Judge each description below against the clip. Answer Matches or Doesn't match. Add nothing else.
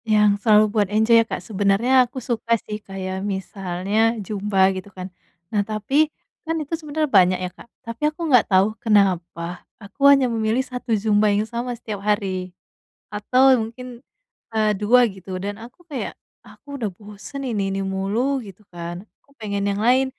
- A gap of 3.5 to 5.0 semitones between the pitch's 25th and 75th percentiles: Matches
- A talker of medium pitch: Doesn't match